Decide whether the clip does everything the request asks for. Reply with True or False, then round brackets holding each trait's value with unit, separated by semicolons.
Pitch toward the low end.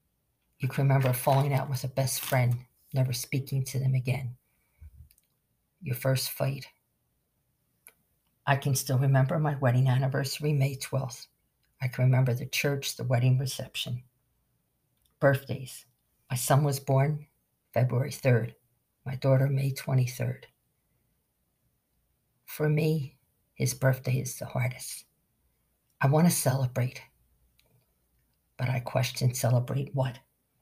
True (130 Hz)